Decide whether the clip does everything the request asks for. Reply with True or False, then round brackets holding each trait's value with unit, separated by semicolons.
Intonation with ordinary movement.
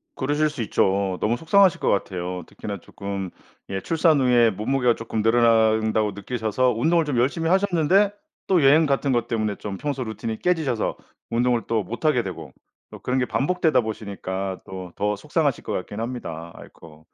False (5.9 semitones)